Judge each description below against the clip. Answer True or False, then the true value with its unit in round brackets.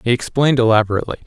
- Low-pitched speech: True (120 Hz)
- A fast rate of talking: False (140 wpm)